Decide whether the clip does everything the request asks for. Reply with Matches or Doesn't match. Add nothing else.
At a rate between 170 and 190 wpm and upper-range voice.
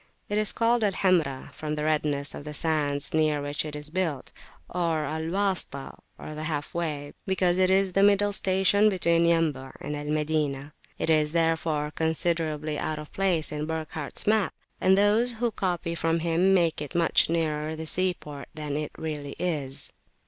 Doesn't match